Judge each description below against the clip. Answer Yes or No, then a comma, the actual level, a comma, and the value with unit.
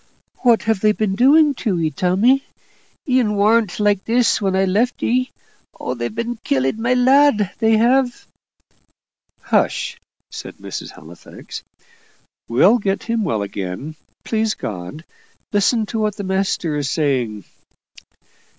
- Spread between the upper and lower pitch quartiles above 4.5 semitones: Yes, wide, 5.5 semitones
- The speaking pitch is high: Yes, high, 210 Hz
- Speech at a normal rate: No, slow, 130 wpm